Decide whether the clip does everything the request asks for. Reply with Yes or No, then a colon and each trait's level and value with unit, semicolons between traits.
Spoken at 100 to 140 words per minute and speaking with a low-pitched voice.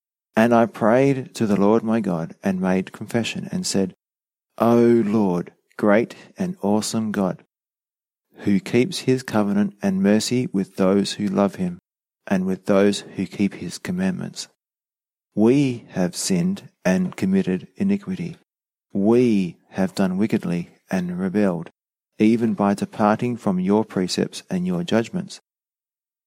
Yes: slow, 135 wpm; low, 115 Hz